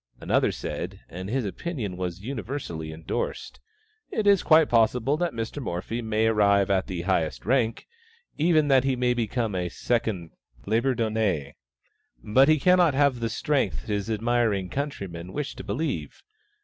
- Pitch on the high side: No, low, 115 Hz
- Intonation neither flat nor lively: No, wide, 5.8 semitones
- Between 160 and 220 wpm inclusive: No, average, 150 wpm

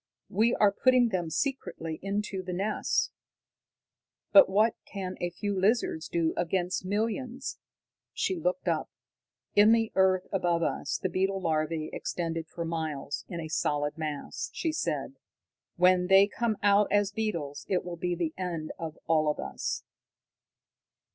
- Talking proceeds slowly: No, average, 150 wpm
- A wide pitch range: No, average, 4.0 semitones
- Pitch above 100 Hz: Yes, medium, 185 Hz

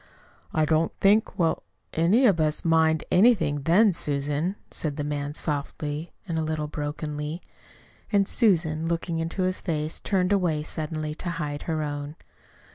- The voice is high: No, medium, 160 Hz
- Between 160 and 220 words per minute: No, average, 145 wpm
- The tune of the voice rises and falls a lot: No, average, 2.7 semitones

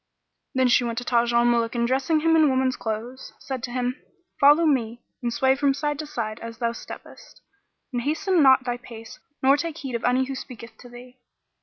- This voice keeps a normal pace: No, fast, 210 wpm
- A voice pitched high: Yes, very high, 255 Hz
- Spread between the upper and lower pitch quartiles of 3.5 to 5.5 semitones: No, average, 2.8 semitones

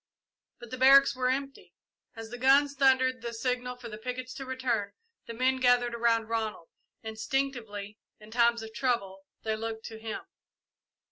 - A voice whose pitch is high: Yes, high, 240 Hz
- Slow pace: No, average, 160 wpm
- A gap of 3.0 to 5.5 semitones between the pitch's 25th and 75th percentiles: No, narrow, 2.6 semitones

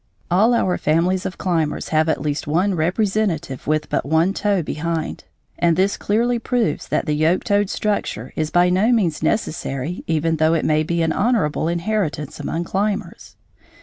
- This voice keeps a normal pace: Yes, average, 170 wpm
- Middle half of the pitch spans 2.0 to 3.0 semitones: No, average, 4.4 semitones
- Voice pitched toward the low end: No, medium, 170 Hz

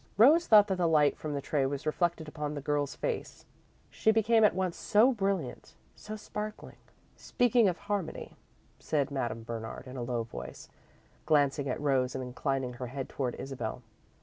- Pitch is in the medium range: Yes, medium, 150 Hz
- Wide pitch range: Yes, wide, 7.4 semitones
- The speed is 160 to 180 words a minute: Yes, average, 175 wpm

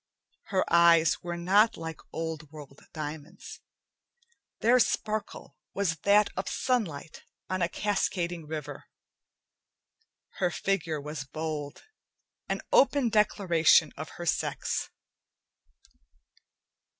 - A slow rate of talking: Yes, slow, 100 wpm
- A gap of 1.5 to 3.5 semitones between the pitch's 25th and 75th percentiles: No, average, 4.4 semitones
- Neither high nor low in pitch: Yes, medium, 170 Hz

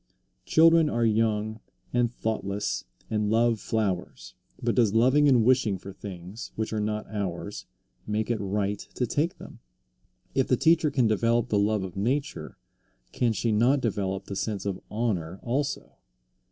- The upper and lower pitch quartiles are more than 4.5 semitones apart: No, average, 3.2 semitones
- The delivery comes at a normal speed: Yes, average, 155 wpm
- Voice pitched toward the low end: Yes, low, 110 Hz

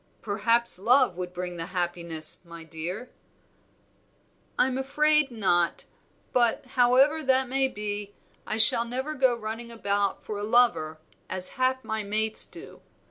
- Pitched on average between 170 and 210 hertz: No, high, 220 Hz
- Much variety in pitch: Yes, wide, 5.8 semitones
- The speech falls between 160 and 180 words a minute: No, slow, 135 wpm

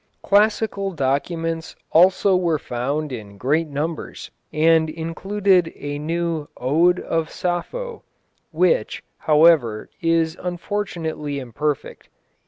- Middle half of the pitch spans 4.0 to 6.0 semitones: No, average, 3.3 semitones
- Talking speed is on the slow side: Yes, slow, 95 wpm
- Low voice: No, medium, 165 Hz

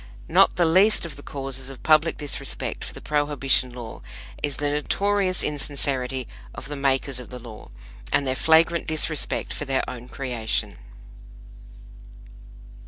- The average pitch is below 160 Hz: Yes, medium, 140 Hz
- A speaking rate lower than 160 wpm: Yes, average, 145 wpm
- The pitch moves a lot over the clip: No, average, 3.2 semitones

